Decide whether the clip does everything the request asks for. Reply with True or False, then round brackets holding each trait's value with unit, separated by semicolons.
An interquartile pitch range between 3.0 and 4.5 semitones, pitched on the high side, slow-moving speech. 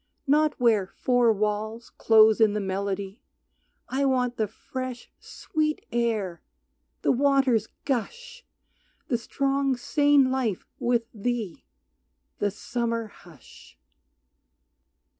True (3.8 semitones; 235 Hz; 105 wpm)